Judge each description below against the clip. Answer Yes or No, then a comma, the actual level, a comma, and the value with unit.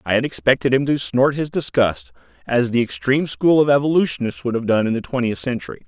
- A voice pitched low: Yes, low, 125 Hz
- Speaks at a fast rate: Yes, fast, 215 wpm